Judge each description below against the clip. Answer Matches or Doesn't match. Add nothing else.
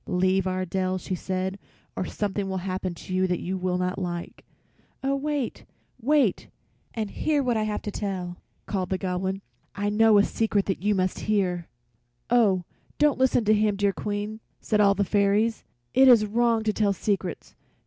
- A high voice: Matches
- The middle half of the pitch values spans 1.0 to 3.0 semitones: Matches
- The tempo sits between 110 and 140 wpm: Doesn't match